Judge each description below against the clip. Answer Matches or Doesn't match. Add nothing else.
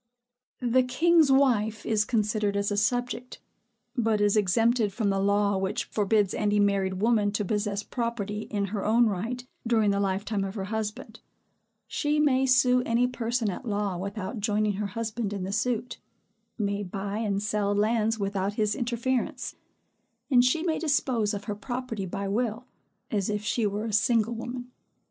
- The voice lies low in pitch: Doesn't match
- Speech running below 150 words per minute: Doesn't match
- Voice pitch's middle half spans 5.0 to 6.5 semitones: Doesn't match